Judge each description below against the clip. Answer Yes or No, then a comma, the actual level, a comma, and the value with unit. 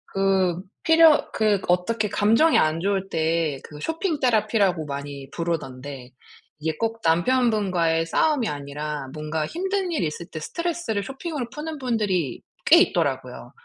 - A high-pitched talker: Yes, high, 195 Hz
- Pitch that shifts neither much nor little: No, wide, 8.2 semitones